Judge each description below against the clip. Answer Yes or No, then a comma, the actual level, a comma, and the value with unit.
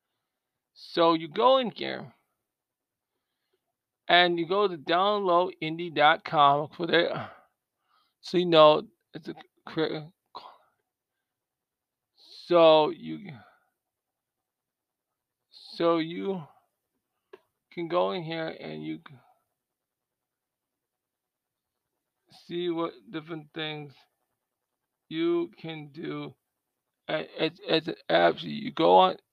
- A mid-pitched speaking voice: Yes, medium, 160 Hz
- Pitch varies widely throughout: Yes, wide, 6.0 semitones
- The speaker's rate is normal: No, slow, 90 wpm